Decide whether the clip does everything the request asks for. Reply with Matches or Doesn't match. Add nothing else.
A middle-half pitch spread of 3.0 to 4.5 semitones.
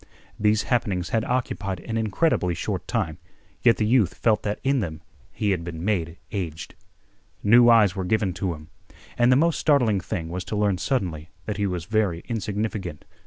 Matches